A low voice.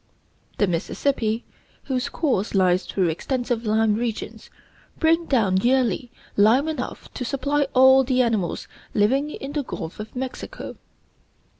No: high, 245 Hz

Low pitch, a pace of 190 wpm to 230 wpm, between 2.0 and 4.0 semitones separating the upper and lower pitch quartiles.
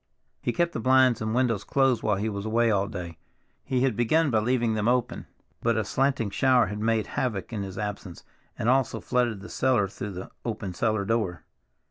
Yes: low, 115 Hz; average, 200 wpm; average, 3.5 semitones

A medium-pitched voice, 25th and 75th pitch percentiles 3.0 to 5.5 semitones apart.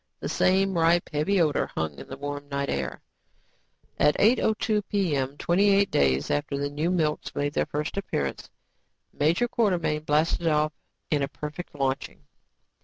Yes: medium, 150 Hz; average, 4.1 semitones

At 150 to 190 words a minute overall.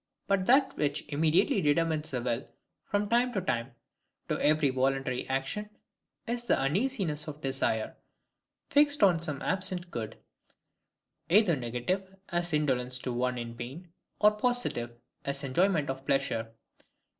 No: slow, 135 wpm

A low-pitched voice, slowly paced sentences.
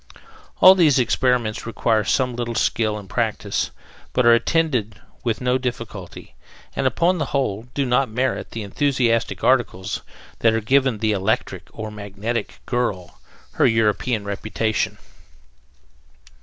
Yes: low, 115 Hz; slow, 130 wpm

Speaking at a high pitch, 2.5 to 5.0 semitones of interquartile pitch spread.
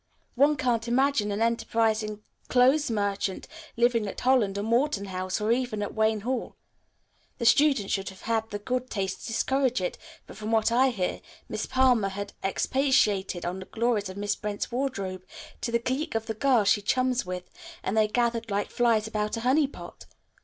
Yes: high, 225 Hz; average, 3.7 semitones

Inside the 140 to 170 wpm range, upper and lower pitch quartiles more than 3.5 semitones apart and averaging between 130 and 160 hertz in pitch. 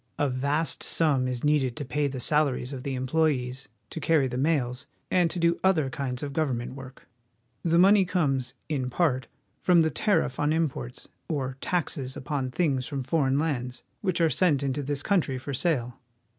No: average, 180 wpm; average, 3.9 semitones; medium, 140 Hz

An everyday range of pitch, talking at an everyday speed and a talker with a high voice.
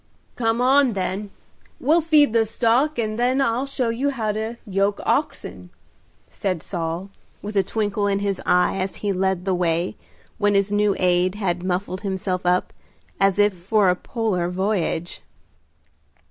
Yes: average, 3.6 semitones; average, 160 wpm; high, 200 Hz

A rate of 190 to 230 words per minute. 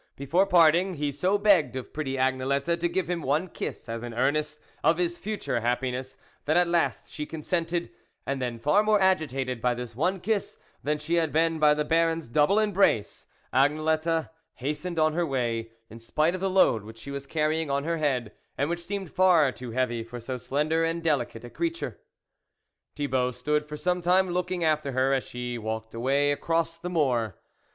Yes: average, 195 wpm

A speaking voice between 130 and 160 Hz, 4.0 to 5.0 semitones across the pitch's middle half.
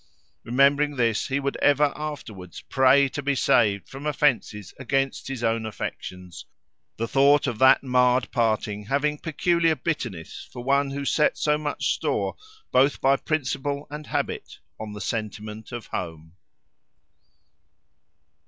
Yes: low, 135 Hz; average, 4.4 semitones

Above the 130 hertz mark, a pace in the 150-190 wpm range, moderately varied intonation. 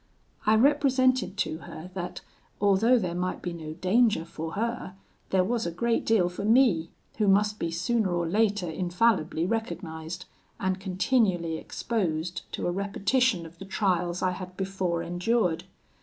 Yes: medium, 185 Hz; average, 155 wpm; average, 4.2 semitones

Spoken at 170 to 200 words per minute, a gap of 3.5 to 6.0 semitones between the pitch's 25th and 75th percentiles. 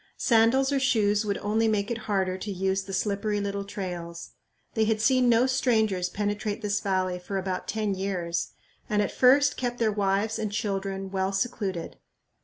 No: average, 175 wpm; narrow, 2.5 semitones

